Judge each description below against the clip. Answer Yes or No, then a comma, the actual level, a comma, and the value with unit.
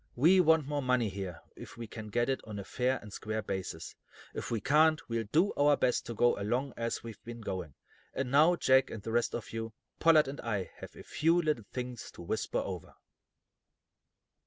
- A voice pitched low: Yes, low, 120 Hz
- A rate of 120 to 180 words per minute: No, fast, 205 wpm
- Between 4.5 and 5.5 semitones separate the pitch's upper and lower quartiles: Yes, average, 4.8 semitones